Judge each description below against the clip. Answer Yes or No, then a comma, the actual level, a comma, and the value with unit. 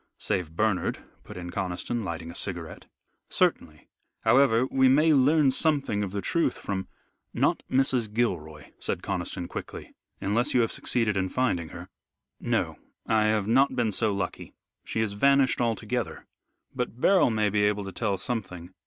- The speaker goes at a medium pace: Yes, average, 160 wpm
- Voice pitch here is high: No, low, 110 Hz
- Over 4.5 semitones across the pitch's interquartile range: Yes, average, 5.0 semitones